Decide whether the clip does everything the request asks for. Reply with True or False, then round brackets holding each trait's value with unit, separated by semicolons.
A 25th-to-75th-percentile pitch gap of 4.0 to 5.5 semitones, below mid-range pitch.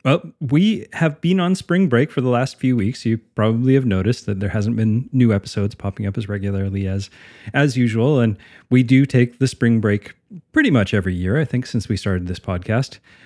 True (4.6 semitones; 120 Hz)